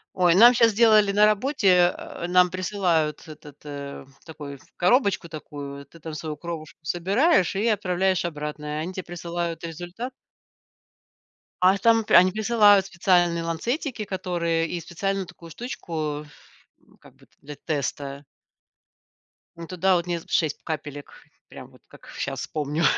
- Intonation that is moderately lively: Yes, average, 4.0 semitones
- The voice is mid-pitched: Yes, medium, 175 Hz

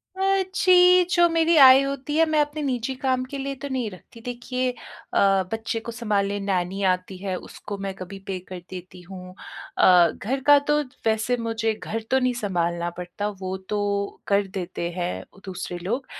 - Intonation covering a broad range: Yes, wide, 5.9 semitones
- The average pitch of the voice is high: Yes, high, 220 Hz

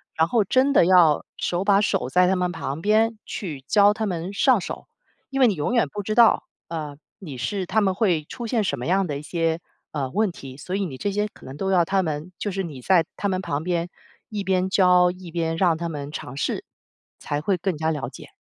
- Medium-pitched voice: Yes, medium, 180 Hz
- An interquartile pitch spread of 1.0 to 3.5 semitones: No, average, 4.0 semitones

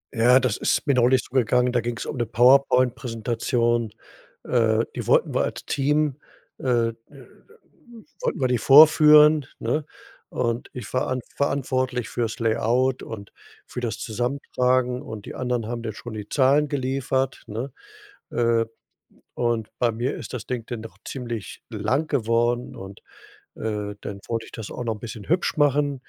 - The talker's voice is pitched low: Yes, low, 120 Hz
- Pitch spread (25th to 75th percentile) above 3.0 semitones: No, narrow, 2.5 semitones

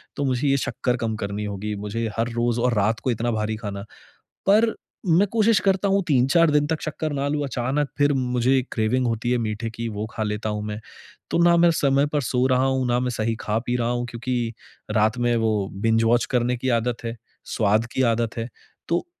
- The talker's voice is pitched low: Yes, low, 120 Hz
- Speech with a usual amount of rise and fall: Yes, average, 3.5 semitones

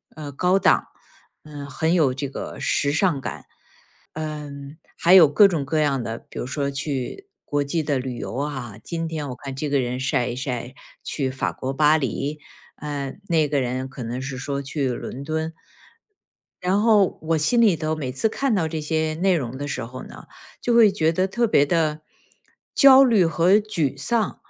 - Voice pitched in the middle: Yes, medium, 150 Hz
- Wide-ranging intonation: No, average, 3.6 semitones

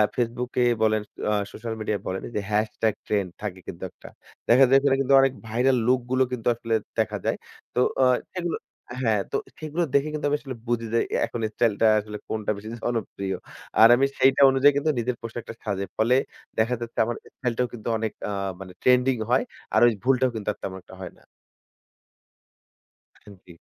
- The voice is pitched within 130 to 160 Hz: No, low, 120 Hz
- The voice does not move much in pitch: No, average, 3.2 semitones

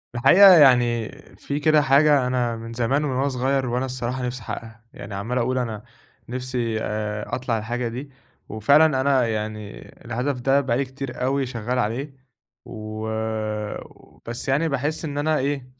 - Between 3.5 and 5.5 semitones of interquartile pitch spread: No, average, 3.1 semitones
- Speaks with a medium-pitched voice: No, low, 125 Hz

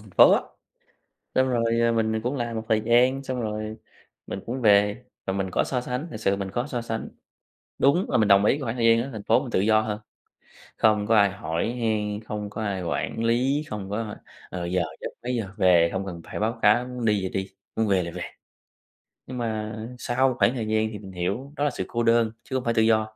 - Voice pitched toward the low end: Yes, low, 110 Hz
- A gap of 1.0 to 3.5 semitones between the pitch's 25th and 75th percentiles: Yes, average, 2.8 semitones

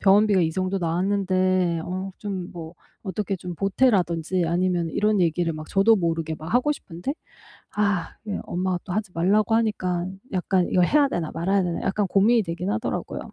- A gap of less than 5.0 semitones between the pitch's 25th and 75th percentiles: Yes, average, 2.8 semitones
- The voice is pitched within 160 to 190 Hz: Yes, medium, 185 Hz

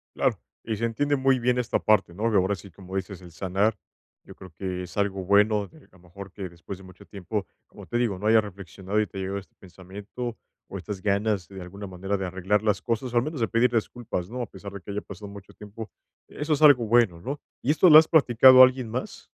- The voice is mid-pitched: No, low, 105 Hz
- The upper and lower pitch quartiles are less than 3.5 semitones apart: No, average, 3.8 semitones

